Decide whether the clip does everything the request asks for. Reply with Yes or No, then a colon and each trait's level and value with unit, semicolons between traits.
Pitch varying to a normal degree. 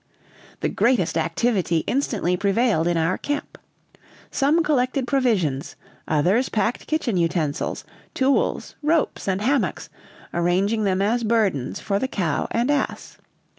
No: wide, 6.7 semitones